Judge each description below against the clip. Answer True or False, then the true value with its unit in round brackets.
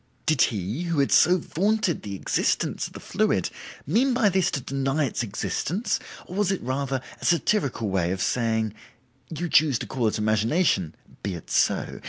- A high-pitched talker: False (135 Hz)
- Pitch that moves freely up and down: True (8.2 semitones)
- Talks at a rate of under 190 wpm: True (180 wpm)